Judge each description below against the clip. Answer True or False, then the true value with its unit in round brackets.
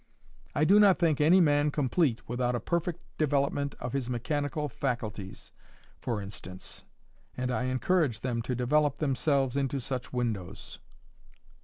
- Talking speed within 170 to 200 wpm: False (140 wpm)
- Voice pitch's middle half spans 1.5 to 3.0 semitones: False (3.5 semitones)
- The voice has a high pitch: False (135 Hz)